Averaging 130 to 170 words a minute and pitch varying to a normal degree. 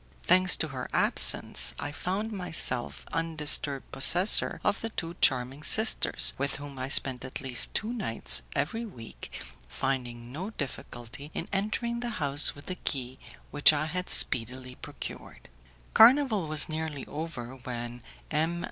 No: average, 145 wpm; wide, 6.0 semitones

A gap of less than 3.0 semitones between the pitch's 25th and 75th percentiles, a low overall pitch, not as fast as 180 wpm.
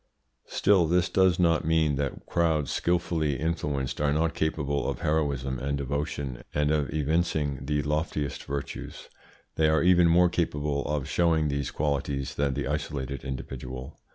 Yes: narrow, 2.5 semitones; very low, 75 Hz; average, 150 wpm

